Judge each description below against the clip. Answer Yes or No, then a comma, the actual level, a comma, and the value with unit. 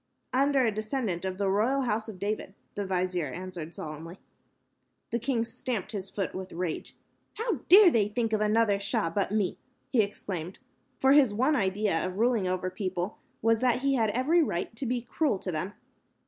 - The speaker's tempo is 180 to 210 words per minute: Yes, average, 190 wpm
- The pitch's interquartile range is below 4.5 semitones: No, average, 4.8 semitones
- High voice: Yes, high, 210 Hz